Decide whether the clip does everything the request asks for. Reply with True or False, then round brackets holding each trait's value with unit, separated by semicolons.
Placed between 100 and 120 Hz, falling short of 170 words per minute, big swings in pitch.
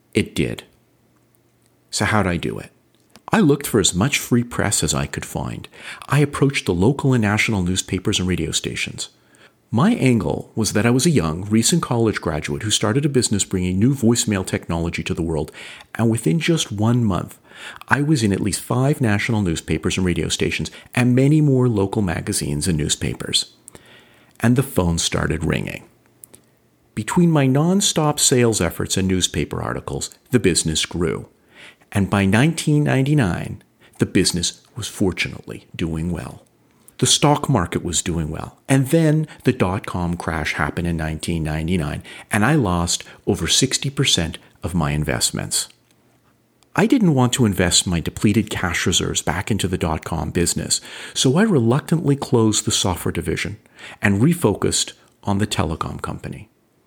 True (105 Hz; 155 wpm; 6.7 semitones)